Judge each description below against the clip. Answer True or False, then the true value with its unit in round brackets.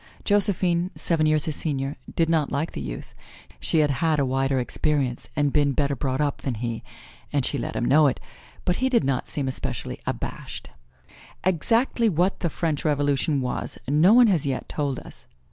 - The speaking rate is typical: True (185 wpm)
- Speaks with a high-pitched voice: False (150 Hz)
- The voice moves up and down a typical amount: True (3.7 semitones)